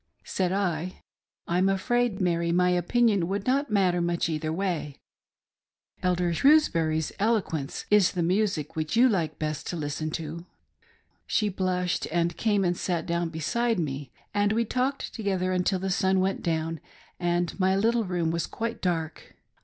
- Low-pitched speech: No, medium, 180 Hz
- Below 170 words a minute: Yes, average, 160 wpm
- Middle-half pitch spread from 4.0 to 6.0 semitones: No, average, 3.3 semitones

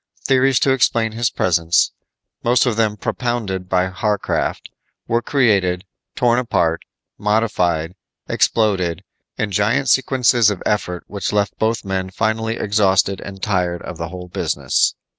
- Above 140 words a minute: No, slow, 135 wpm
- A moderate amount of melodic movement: Yes, average, 4.0 semitones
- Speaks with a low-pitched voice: Yes, low, 105 Hz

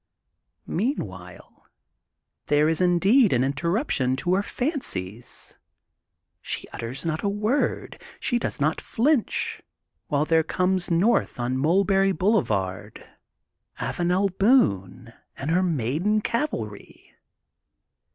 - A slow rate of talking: Yes, slow, 105 wpm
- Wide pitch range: Yes, wide, 7.8 semitones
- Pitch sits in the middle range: Yes, medium, 170 Hz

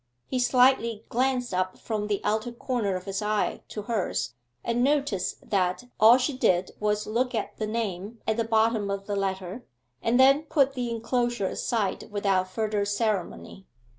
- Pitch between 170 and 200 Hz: No, high, 220 Hz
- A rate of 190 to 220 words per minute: No, average, 165 wpm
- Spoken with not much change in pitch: No, average, 3.5 semitones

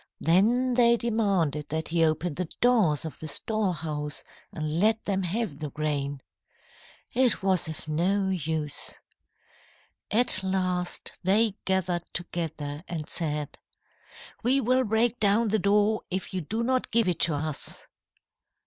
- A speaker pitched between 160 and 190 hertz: Yes, medium, 185 Hz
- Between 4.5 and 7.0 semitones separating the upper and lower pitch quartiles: Yes, wide, 5.6 semitones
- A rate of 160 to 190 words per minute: No, average, 140 wpm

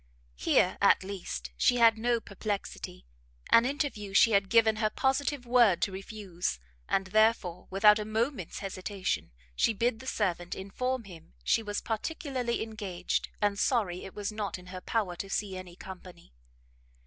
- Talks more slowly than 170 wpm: Yes, average, 160 wpm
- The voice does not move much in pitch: No, average, 3.6 semitones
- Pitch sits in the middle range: No, high, 205 Hz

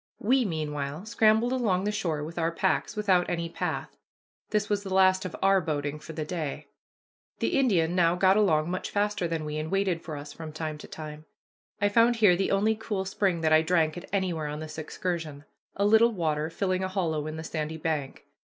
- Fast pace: Yes, fast, 210 wpm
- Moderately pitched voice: Yes, medium, 175 Hz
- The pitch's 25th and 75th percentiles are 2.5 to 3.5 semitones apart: No, average, 4.1 semitones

